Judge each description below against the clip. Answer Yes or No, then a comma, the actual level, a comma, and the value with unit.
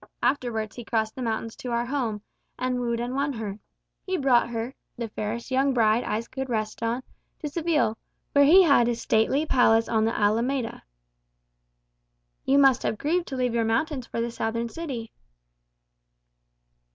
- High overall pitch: Yes, high, 240 Hz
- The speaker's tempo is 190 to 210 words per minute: No, average, 165 wpm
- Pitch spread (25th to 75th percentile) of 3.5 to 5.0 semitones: No, average, 3.1 semitones